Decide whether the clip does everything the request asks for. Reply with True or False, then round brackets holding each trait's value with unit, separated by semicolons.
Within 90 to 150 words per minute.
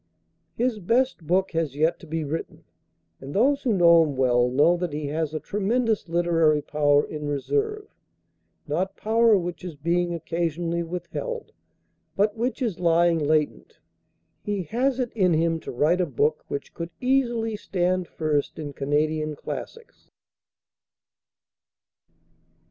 True (140 wpm)